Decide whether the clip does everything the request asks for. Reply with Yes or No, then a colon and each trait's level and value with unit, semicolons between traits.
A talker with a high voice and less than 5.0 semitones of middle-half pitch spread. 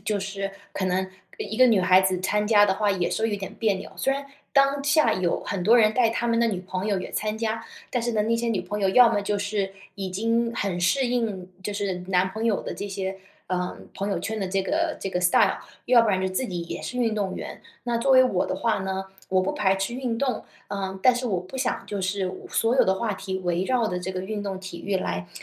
Yes: high, 200 Hz; average, 3.5 semitones